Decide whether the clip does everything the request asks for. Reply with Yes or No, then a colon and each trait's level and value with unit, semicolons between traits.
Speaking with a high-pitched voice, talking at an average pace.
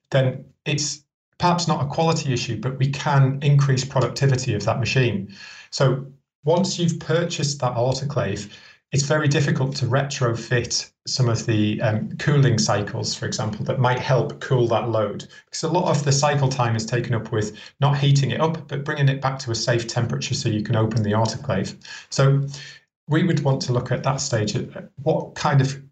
No: low, 135 Hz; average, 190 wpm